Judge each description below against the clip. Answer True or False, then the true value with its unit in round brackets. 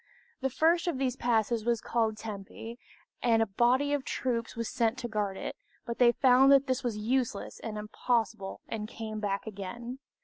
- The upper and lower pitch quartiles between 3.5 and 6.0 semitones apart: False (2.9 semitones)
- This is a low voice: False (235 Hz)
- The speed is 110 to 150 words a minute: False (180 wpm)